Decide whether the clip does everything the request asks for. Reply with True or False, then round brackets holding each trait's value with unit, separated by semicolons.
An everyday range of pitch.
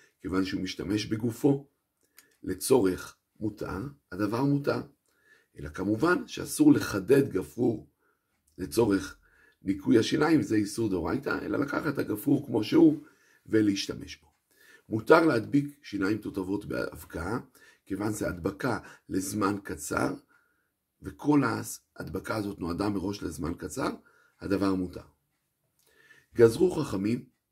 False (6.4 semitones)